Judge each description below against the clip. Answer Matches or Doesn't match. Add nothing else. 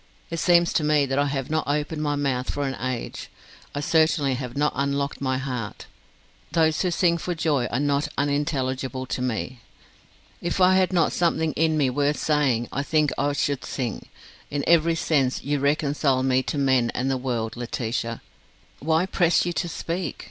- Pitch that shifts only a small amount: Doesn't match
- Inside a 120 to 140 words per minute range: Doesn't match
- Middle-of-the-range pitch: Matches